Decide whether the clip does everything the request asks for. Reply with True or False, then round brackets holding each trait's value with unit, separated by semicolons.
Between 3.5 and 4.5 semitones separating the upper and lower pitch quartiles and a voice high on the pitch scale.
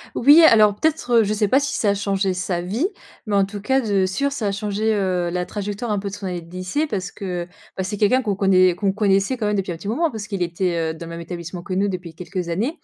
False (2.9 semitones; 200 Hz)